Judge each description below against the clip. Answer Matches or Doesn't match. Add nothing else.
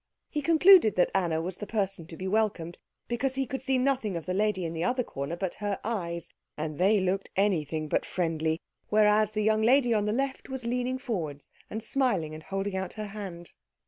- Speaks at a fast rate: Matches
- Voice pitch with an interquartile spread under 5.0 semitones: Doesn't match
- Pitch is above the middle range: Matches